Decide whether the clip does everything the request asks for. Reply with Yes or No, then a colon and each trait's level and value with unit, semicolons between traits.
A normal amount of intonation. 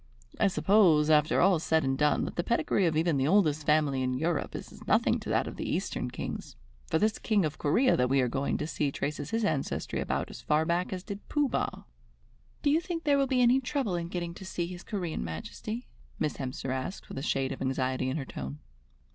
No: wide, 6.6 semitones